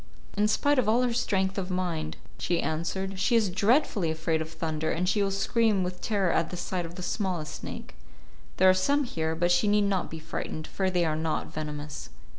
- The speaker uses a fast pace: Yes, fast, 215 wpm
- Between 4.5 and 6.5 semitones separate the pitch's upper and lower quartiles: No, average, 4.1 semitones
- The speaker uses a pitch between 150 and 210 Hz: Yes, medium, 185 Hz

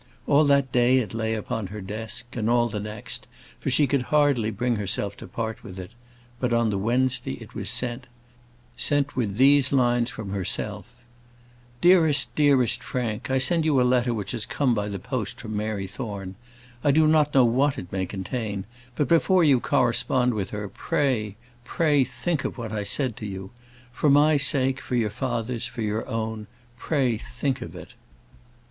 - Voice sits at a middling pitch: No, low, 120 Hz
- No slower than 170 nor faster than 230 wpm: Yes, average, 185 wpm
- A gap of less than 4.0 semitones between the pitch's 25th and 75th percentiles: No, average, 4.3 semitones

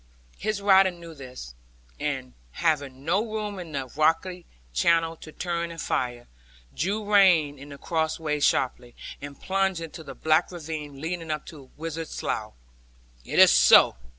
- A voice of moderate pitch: Yes, medium, 160 Hz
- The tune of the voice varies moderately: Yes, average, 4.0 semitones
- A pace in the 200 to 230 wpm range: No, average, 150 wpm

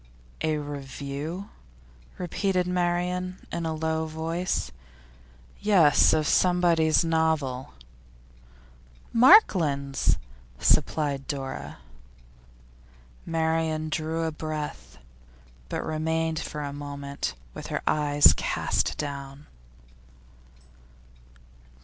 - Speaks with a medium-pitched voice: Yes, medium, 160 Hz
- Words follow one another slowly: Yes, slow, 80 wpm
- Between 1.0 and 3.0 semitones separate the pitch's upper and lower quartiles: Yes, narrow, 2.5 semitones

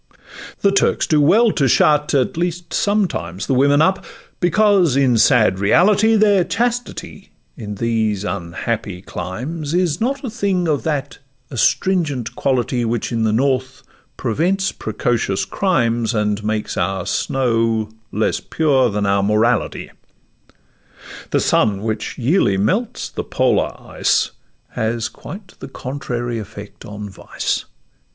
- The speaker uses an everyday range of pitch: No, wide, 8.3 semitones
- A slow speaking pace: Yes, slow, 130 wpm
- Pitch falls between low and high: No, low, 130 Hz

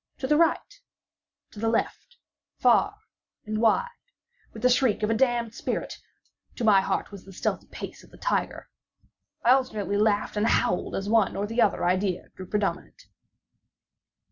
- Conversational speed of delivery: Yes, average, 155 wpm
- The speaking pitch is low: No, high, 220 Hz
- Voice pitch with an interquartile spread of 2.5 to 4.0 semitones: Yes, average, 3.7 semitones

